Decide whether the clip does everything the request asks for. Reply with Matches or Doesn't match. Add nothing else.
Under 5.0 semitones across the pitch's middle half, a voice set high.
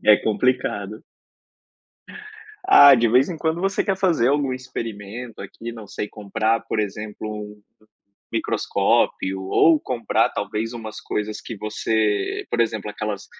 Doesn't match